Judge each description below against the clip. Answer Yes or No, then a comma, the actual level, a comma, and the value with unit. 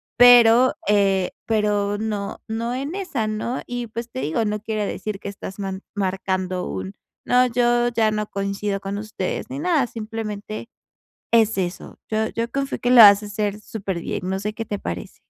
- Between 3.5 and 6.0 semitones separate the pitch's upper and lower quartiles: No, average, 2.8 semitones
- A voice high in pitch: Yes, high, 215 Hz